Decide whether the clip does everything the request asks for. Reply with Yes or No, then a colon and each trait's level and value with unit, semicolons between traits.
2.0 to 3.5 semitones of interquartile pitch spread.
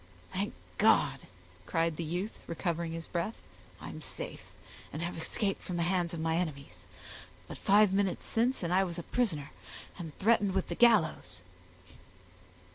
Yes: average, 3.0 semitones